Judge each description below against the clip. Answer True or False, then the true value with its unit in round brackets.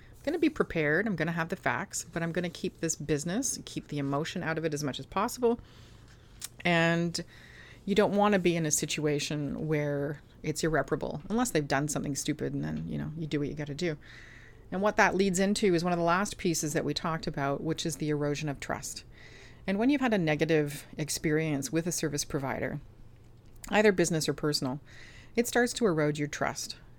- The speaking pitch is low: False (155 Hz)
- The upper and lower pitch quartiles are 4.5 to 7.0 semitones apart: False (3.9 semitones)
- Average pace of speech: False (215 wpm)